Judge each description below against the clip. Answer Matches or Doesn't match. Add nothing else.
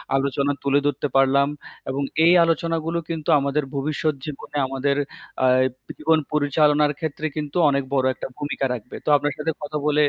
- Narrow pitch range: Matches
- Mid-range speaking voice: Matches